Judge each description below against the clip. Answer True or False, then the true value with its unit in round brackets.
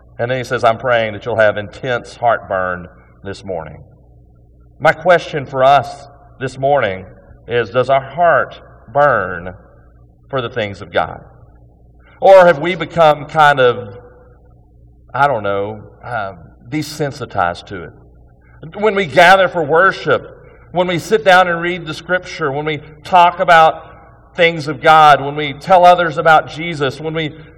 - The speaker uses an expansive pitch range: True (8.4 semitones)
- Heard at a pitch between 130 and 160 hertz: True (140 Hz)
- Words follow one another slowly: False (150 wpm)